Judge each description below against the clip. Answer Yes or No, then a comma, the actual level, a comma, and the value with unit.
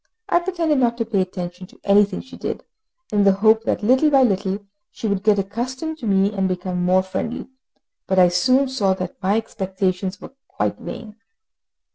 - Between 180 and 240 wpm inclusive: Yes, average, 185 wpm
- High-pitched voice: Yes, high, 200 Hz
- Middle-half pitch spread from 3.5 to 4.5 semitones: Yes, average, 4.2 semitones